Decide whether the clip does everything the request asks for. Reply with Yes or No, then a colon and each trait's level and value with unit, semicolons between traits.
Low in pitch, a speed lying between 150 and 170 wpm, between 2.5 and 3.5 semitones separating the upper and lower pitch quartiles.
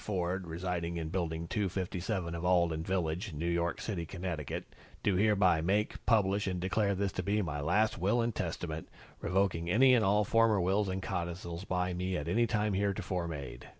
No: very low, 90 Hz; average, 180 wpm; average, 3.0 semitones